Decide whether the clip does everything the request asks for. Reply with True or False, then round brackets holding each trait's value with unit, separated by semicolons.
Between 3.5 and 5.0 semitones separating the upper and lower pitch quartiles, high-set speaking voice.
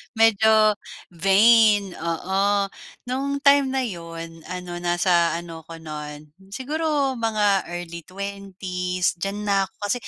True (4.2 semitones; 195 Hz)